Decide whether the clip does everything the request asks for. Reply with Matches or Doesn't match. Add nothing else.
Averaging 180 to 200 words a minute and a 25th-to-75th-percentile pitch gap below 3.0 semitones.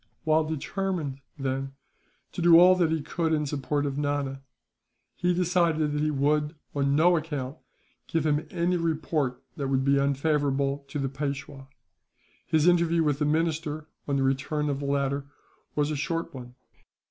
Doesn't match